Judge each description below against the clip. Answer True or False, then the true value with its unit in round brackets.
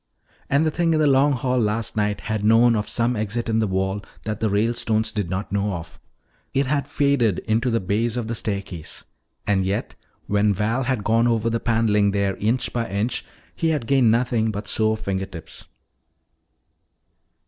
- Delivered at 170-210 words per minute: True (185 wpm)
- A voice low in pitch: True (110 Hz)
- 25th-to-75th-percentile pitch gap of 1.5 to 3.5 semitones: True (2.9 semitones)